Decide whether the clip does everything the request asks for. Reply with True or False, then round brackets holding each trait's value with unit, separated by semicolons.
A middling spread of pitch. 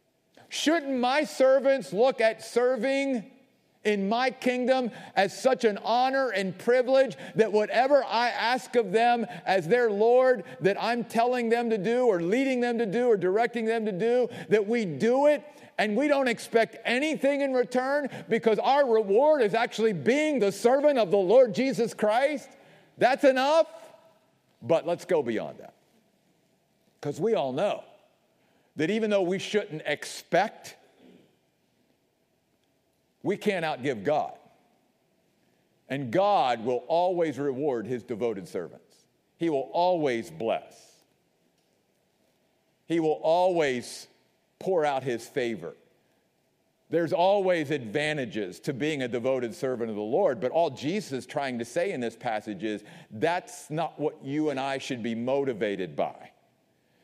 False (7.6 semitones)